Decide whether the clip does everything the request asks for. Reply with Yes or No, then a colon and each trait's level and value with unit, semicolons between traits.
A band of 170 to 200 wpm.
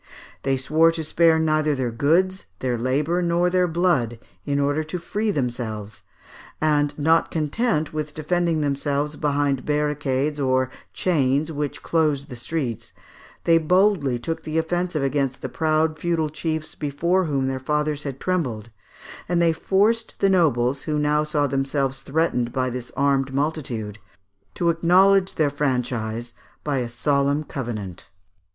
No: average, 145 wpm